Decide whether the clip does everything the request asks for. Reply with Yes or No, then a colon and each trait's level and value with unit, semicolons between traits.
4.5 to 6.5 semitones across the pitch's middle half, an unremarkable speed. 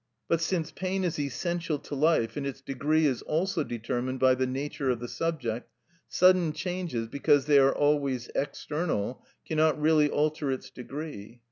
No: average, 3.6 semitones; average, 160 wpm